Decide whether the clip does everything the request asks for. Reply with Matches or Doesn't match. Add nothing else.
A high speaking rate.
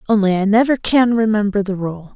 Doesn't match